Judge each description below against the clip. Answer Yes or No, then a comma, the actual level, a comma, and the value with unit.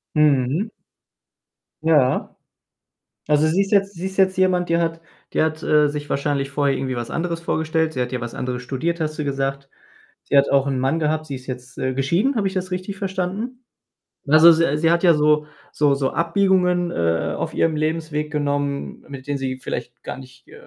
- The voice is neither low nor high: Yes, medium, 150 Hz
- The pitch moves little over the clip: No, average, 3.8 semitones